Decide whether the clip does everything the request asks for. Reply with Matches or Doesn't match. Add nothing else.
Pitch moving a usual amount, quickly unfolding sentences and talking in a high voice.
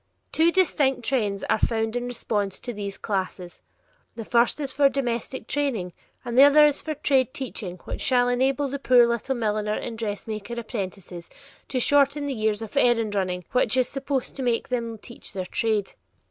Doesn't match